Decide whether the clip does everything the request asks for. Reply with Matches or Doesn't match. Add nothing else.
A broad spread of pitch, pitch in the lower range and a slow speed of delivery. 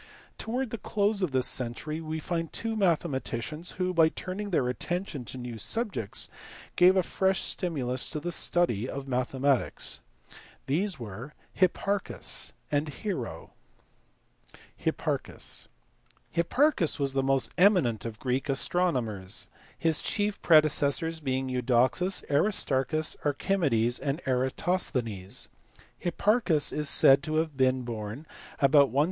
Doesn't match